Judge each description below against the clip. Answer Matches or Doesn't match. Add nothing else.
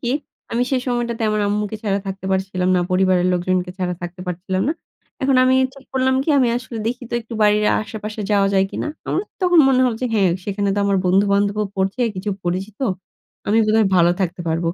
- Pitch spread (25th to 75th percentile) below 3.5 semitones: Doesn't match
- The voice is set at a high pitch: Matches